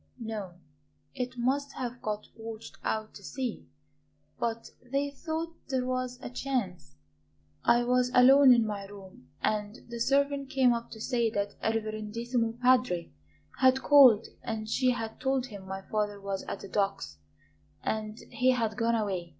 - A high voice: Yes, high, 230 Hz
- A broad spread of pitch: No, average, 3.3 semitones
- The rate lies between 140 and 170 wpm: Yes, average, 160 wpm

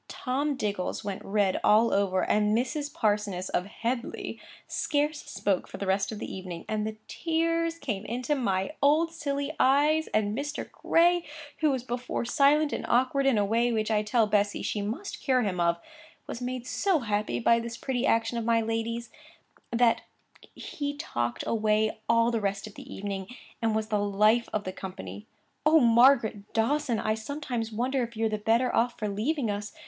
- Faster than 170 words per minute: Yes, average, 185 wpm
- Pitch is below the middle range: No, high, 230 Hz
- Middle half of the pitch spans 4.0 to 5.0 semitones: Yes, average, 4.5 semitones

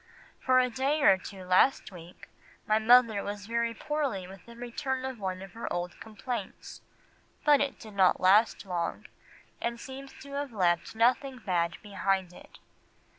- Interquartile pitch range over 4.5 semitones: Yes, average, 5.2 semitones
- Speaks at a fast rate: No, average, 165 wpm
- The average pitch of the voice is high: Yes, high, 220 Hz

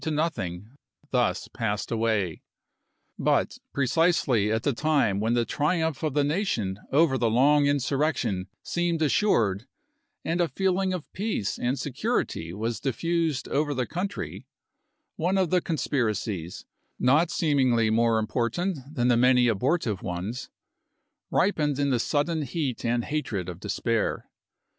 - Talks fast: No, slow, 135 wpm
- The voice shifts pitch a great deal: Yes, wide, 6.0 semitones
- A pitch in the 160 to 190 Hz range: No, low, 130 Hz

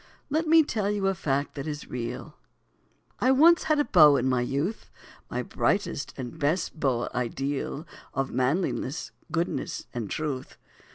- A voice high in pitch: No, medium, 150 Hz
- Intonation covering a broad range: Yes, wide, 7.0 semitones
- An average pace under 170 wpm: Yes, average, 155 wpm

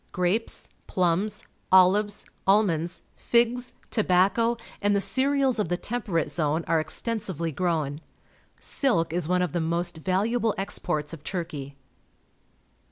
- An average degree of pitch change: Yes, average, 4.5 semitones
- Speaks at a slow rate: Yes, slow, 130 wpm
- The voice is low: No, medium, 185 Hz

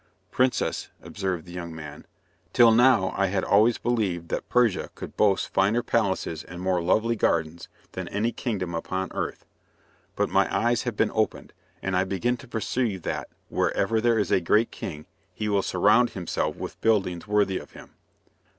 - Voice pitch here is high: No, low, 100 Hz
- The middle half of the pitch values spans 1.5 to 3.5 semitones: No, average, 4.0 semitones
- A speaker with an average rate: Yes, average, 170 wpm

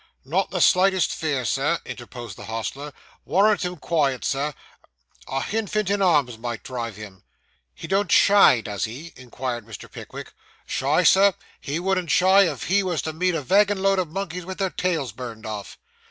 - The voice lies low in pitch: No, medium, 160 Hz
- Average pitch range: No, wide, 7.3 semitones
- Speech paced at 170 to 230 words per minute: Yes, average, 175 wpm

